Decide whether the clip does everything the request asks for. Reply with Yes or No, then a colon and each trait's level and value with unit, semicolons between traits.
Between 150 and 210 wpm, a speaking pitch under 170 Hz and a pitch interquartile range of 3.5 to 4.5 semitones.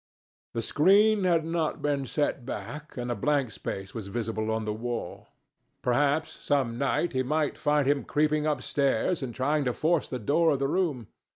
Yes: average, 180 wpm; medium, 140 Hz; average, 4.1 semitones